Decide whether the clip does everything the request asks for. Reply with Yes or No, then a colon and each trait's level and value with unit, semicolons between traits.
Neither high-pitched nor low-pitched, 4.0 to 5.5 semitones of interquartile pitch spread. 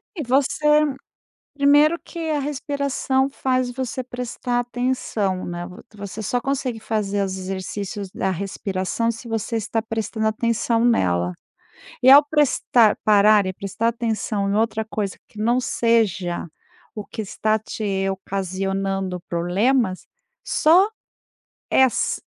No: high, 220 Hz; average, 4.3 semitones